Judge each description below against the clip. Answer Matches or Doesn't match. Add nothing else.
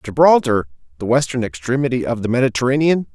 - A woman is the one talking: Doesn't match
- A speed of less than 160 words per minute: Matches